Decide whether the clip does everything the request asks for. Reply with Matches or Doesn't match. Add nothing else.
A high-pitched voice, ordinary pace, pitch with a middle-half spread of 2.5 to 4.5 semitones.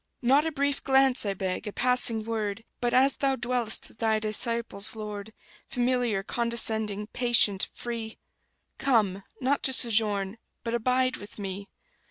Matches